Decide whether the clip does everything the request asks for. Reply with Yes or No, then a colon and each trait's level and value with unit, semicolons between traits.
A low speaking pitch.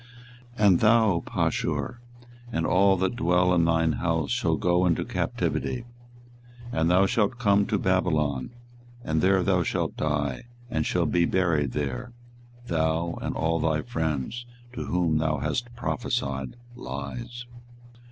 Yes: very low, 85 Hz